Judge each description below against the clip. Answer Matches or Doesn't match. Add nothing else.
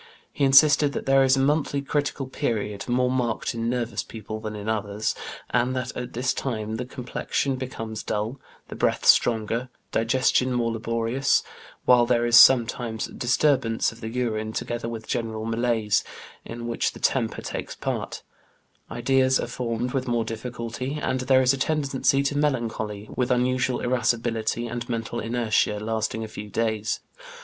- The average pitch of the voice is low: Matches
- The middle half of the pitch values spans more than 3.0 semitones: Doesn't match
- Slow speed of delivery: Doesn't match